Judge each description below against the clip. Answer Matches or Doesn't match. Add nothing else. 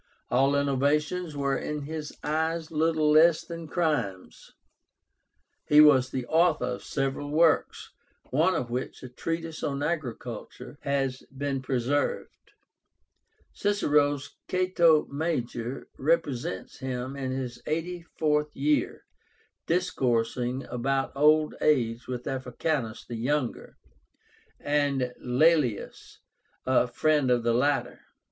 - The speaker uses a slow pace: Matches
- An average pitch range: Matches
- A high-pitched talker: Doesn't match